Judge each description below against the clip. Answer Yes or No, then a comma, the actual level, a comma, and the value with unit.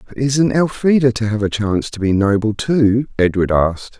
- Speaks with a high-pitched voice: No, low, 115 Hz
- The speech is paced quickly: No, average, 195 wpm